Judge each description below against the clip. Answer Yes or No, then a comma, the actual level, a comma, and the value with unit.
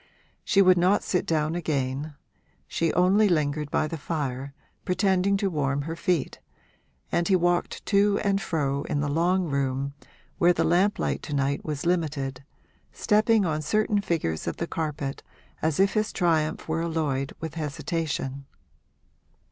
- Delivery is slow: No, average, 155 wpm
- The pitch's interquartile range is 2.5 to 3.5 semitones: No, average, 4.2 semitones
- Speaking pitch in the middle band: Yes, medium, 160 Hz